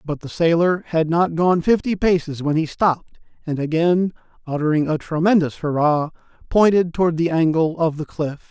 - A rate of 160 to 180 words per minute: Yes, average, 170 wpm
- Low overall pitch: No, medium, 165 Hz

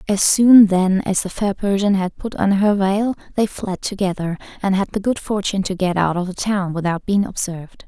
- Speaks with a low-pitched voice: No, high, 195 Hz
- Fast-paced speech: Yes, fast, 220 wpm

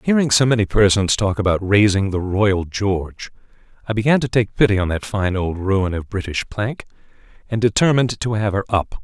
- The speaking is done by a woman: No, male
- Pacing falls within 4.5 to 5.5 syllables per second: Yes, 5.4 syllables/s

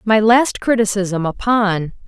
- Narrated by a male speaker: No, female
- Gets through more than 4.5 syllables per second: No, 3.8 syllables/s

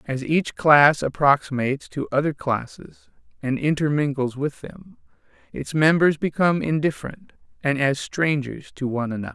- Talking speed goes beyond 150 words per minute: No, slow, 135 wpm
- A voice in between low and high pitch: Yes, medium, 145 Hz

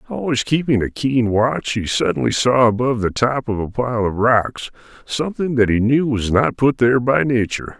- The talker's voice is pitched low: Yes, low, 120 Hz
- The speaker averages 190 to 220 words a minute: Yes, average, 200 wpm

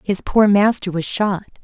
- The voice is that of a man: No, female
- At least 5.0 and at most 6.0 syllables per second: No, 4.4 syllables/s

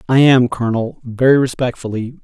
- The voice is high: No, low, 125 Hz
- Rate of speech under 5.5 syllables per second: No, 5.6 syllables/s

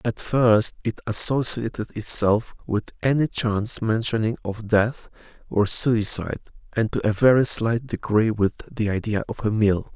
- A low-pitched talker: Yes, low, 110 Hz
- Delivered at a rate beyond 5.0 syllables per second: No, 4.5 syllables/s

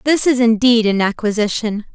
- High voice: Yes, high, 230 Hz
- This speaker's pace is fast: No, average, 155 wpm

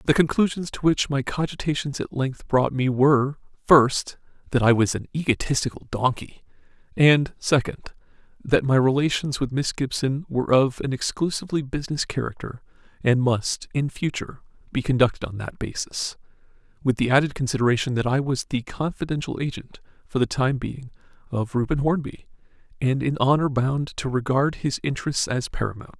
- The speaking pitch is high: No, low, 135 Hz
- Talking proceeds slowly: No, average, 155 wpm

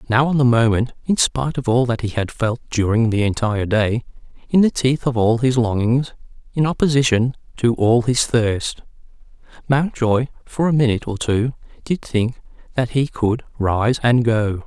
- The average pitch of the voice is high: No, low, 120 Hz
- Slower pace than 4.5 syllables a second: No, 4.8 syllables/s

